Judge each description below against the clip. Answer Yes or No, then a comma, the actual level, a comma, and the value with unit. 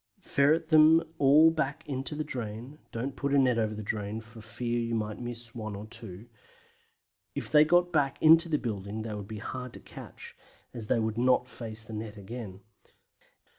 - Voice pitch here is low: Yes, low, 120 Hz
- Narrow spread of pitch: No, average, 4.5 semitones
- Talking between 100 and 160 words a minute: No, average, 190 wpm